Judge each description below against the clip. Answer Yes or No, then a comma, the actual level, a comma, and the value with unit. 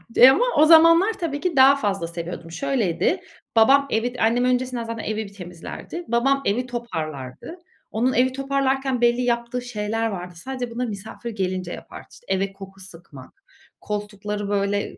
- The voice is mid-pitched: No, high, 230 Hz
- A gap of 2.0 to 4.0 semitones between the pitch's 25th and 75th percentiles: No, average, 5.0 semitones